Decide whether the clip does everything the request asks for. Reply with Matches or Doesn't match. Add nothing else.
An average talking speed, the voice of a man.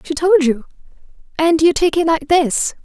Doesn't match